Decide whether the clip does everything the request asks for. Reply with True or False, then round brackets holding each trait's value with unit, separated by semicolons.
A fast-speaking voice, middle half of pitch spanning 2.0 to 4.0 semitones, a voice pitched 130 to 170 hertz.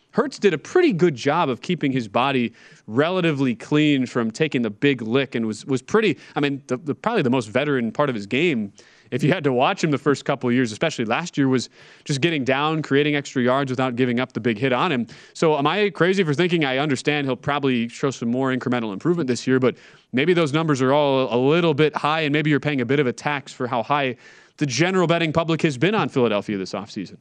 True (245 wpm; 3.7 semitones; 140 Hz)